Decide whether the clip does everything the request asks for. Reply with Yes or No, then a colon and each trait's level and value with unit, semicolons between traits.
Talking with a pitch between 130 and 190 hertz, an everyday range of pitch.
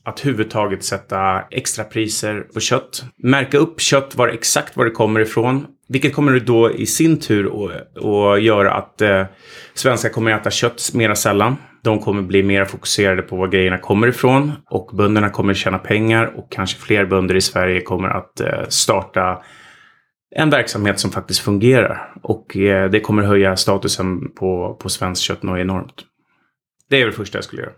No: low, 105 Hz; average, 4.1 semitones